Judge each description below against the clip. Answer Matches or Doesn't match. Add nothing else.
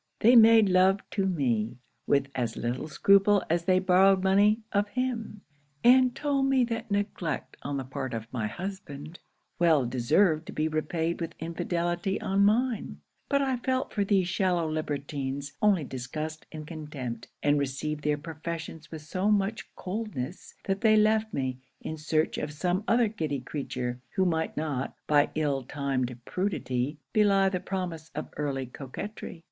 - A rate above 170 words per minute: Doesn't match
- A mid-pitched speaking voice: Matches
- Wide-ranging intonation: Matches